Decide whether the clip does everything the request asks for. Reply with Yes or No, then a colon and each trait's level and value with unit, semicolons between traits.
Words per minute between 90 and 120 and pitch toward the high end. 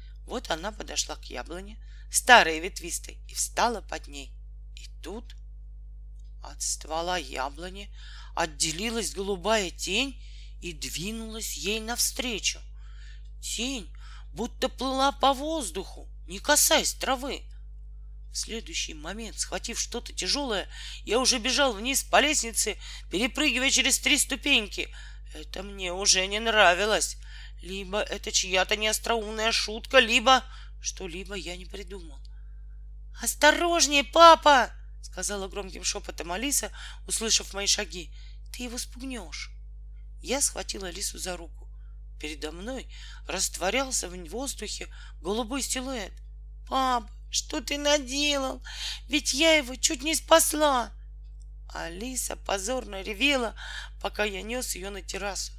Yes: average, 115 wpm; high, 205 Hz